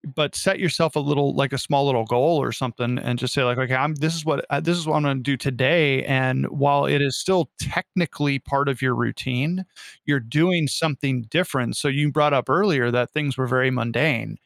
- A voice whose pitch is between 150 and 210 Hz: No, medium, 140 Hz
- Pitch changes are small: No, average, 3.0 semitones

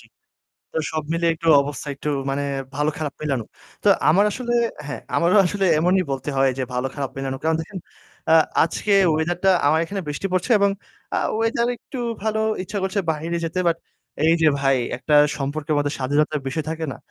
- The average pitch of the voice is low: No, medium, 160 Hz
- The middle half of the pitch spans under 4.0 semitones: No, average, 4.3 semitones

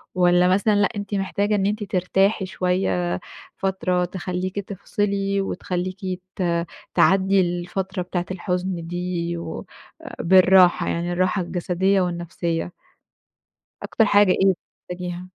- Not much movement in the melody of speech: Yes, narrow, 1.6 semitones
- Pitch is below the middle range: No, medium, 185 Hz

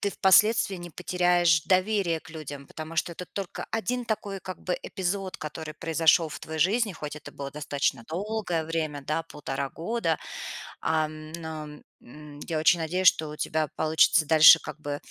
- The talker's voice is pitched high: No, medium, 160 Hz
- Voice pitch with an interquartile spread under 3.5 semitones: Yes, average, 3.1 semitones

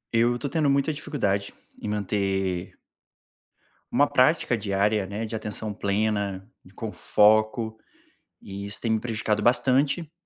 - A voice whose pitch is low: Yes, low, 110 Hz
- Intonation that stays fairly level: No, average, 3.4 semitones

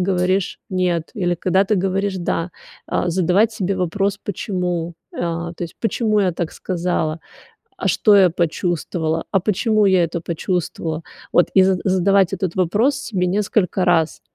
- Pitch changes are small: Yes, narrow, 2.3 semitones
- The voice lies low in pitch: No, medium, 185 Hz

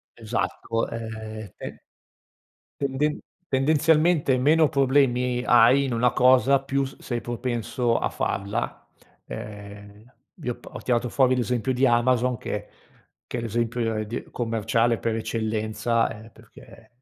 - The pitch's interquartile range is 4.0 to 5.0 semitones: No, average, 2.7 semitones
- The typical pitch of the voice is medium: No, low, 120 Hz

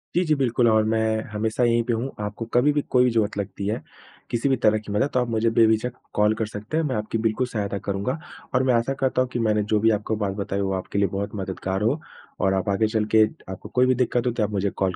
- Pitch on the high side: No, low, 110 Hz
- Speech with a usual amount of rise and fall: Yes, average, 3.1 semitones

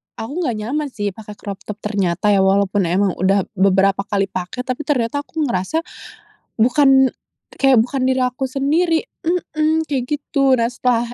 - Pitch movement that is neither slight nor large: No, wide, 5.8 semitones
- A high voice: Yes, high, 245 Hz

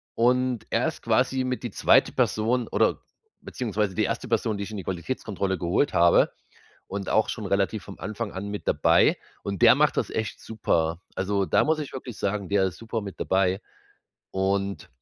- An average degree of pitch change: Yes, average, 3.0 semitones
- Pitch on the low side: Yes, low, 100 Hz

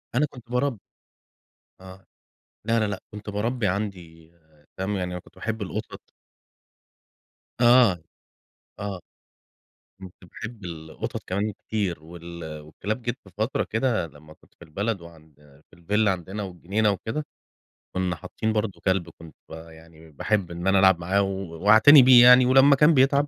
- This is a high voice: No, low, 100 Hz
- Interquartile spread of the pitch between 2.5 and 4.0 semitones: No, average, 4.7 semitones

